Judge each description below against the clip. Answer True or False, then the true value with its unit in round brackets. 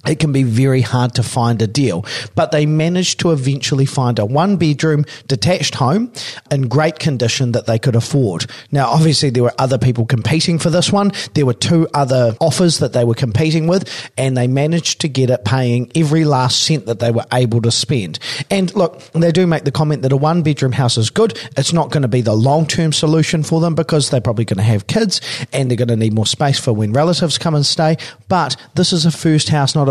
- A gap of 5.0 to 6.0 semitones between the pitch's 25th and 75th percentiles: False (4.5 semitones)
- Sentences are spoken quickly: True (235 wpm)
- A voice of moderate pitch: True (145 Hz)